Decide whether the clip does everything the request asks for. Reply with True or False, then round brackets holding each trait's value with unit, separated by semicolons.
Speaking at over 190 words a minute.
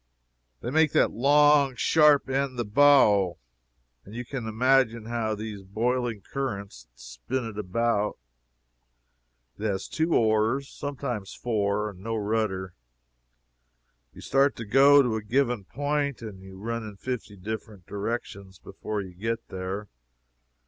False (140 wpm)